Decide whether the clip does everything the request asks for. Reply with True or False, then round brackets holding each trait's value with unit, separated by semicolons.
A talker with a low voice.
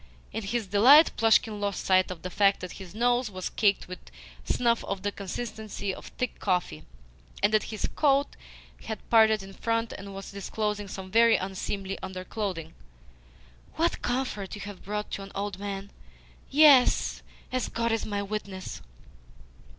False (205 Hz)